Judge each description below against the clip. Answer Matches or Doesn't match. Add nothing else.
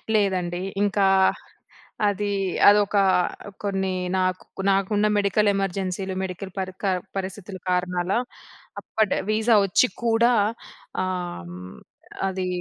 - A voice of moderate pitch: Doesn't match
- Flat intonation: Matches